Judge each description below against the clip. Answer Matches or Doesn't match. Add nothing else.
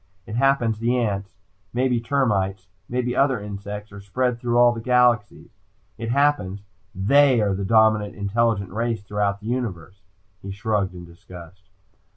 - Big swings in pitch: Doesn't match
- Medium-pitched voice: Doesn't match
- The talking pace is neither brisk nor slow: Matches